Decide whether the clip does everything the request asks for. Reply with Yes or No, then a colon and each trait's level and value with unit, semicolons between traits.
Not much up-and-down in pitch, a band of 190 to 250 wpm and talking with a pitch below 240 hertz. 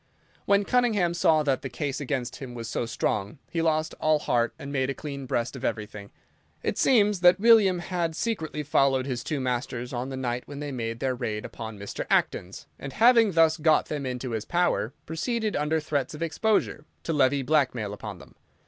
No: average, 5.1 semitones; average, 195 wpm; medium, 140 Hz